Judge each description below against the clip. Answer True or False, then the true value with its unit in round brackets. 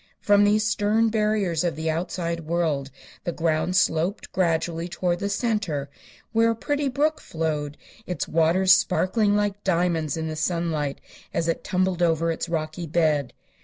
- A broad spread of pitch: False (4.2 semitones)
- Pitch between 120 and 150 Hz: False (175 Hz)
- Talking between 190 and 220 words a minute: False (155 wpm)